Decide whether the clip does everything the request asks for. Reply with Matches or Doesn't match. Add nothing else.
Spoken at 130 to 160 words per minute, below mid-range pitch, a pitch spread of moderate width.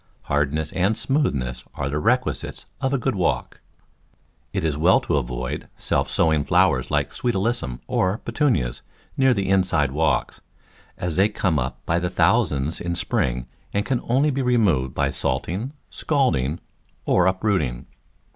Doesn't match